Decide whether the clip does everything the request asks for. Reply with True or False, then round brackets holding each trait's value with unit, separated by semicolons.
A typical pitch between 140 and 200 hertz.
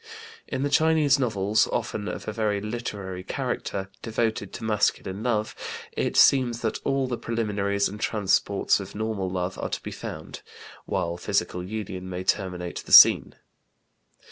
False (105 Hz)